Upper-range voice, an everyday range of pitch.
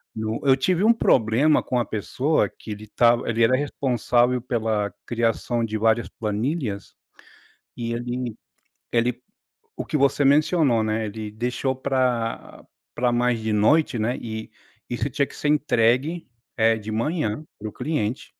No: low, 120 Hz; average, 3.3 semitones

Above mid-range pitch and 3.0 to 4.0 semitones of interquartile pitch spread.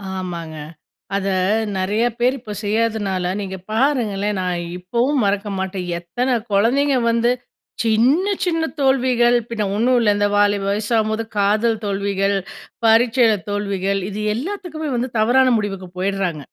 Yes: high, 215 Hz; average, 3.6 semitones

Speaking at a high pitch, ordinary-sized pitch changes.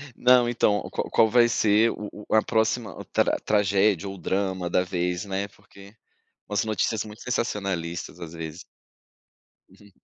No: low, 100 Hz; average, 3.0 semitones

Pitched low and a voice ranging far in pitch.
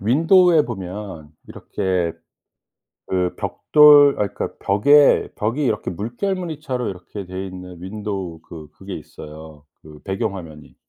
Yes: very low, 95 Hz; wide, 6.4 semitones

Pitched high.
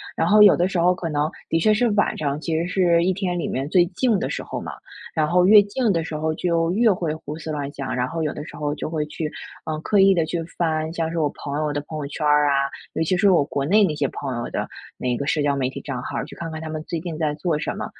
No: medium, 160 Hz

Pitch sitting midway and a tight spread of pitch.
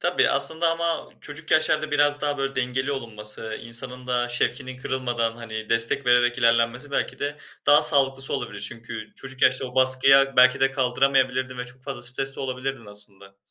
No: low, 130 Hz; narrow, 2.3 semitones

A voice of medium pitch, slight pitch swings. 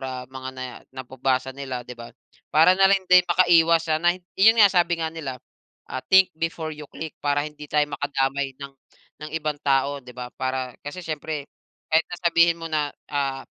No: medium, 150 Hz; average, 4.0 semitones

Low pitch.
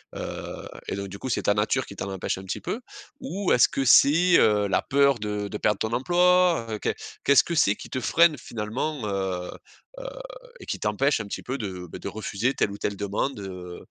Yes: low, 110 Hz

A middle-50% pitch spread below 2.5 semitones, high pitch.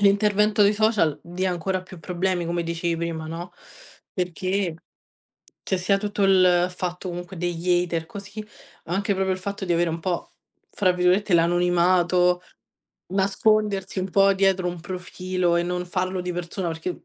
No: narrow, 1.8 semitones; medium, 180 Hz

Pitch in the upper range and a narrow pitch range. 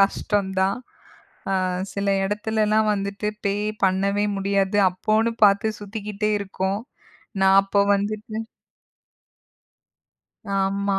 Yes: high, 200 Hz; narrow, 1.4 semitones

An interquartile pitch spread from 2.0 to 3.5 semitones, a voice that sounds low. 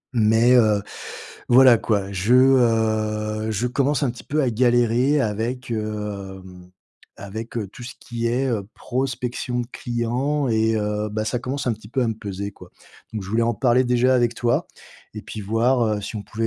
Yes: narrow, 2.6 semitones; low, 115 Hz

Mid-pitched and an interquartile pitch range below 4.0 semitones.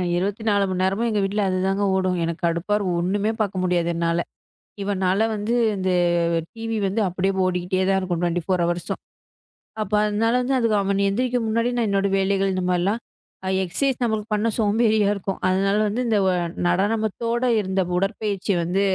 No: high, 195 Hz; average, 2.8 semitones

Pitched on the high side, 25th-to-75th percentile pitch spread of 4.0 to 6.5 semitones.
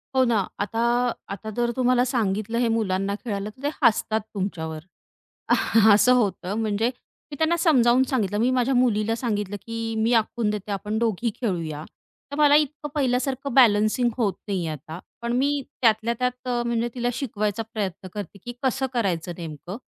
No: high, 225 Hz; average, 3.6 semitones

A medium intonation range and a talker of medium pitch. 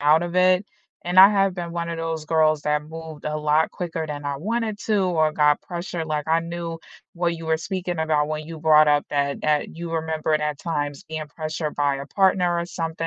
No: narrow, 2.3 semitones; medium, 160 Hz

